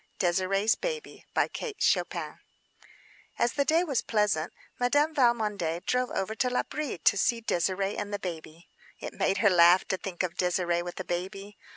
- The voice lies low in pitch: No, high, 195 Hz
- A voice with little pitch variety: No, wide, 5.4 semitones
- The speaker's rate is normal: Yes, average, 155 wpm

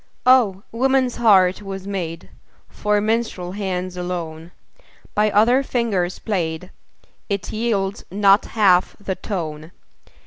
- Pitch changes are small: No, average, 3.2 semitones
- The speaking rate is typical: No, slow, 110 wpm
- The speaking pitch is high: Yes, high, 195 Hz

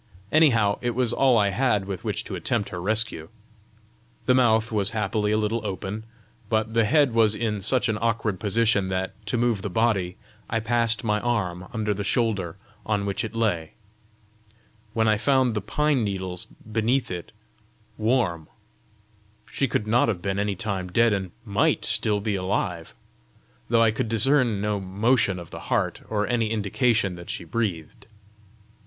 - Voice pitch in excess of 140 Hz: No, low, 110 Hz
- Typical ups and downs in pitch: Yes, average, 3.0 semitones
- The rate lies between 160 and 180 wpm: Yes, average, 170 wpm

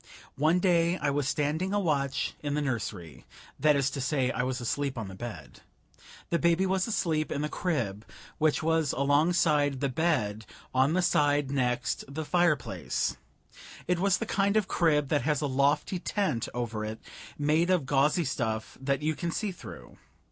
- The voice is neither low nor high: Yes, medium, 145 Hz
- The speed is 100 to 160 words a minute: No, average, 175 wpm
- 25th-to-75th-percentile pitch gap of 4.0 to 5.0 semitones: Yes, average, 4.4 semitones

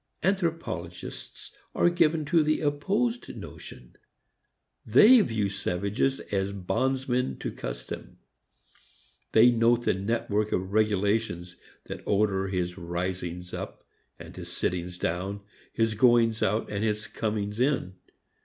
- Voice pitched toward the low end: Yes, low, 105 Hz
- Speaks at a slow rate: Yes, slow, 115 wpm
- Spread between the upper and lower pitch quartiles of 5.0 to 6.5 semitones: Yes, wide, 5.6 semitones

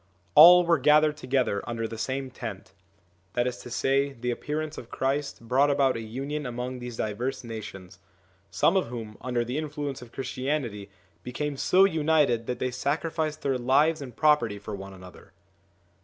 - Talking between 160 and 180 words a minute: Yes, average, 170 wpm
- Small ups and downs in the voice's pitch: No, average, 4.1 semitones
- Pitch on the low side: Yes, low, 130 Hz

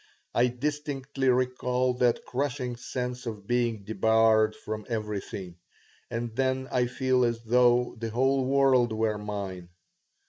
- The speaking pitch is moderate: No, low, 120 Hz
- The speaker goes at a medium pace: No, slow, 130 wpm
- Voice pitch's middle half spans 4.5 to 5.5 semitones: No, narrow, 2.6 semitones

